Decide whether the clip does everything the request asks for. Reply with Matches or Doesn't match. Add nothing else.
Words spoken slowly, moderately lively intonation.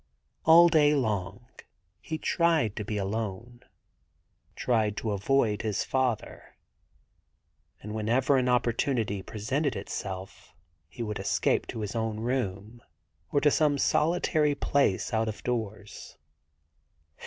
Matches